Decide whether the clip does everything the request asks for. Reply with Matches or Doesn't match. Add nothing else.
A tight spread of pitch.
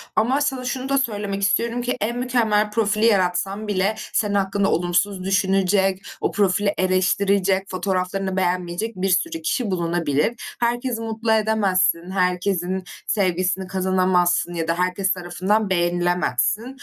Doesn't match